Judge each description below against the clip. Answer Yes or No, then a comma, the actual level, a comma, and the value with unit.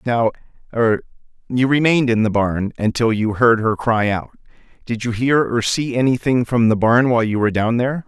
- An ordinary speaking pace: Yes, average, 185 wpm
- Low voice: Yes, low, 120 Hz